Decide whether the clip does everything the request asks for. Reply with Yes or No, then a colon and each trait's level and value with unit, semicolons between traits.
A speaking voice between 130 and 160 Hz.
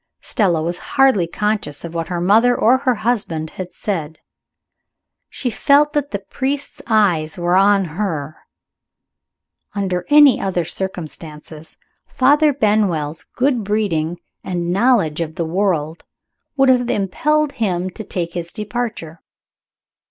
No: high, 195 Hz